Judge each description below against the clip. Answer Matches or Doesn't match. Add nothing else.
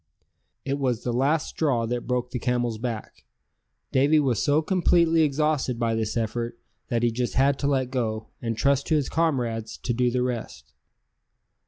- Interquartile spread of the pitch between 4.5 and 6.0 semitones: Doesn't match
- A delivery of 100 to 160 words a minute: Doesn't match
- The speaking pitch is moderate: Doesn't match